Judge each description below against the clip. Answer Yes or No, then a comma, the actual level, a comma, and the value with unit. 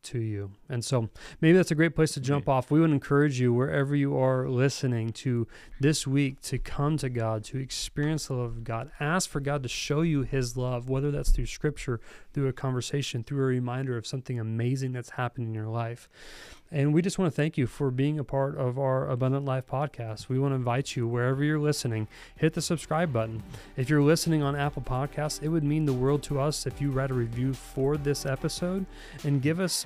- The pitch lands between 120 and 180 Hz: Yes, low, 135 Hz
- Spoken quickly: Yes, fast, 225 wpm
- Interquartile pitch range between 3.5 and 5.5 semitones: No, average, 2.9 semitones